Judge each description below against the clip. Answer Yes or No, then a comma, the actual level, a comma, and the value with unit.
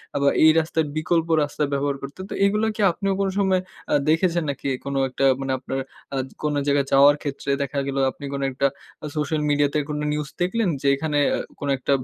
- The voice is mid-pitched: Yes, medium, 145 Hz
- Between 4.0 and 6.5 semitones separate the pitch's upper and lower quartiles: No, average, 2.9 semitones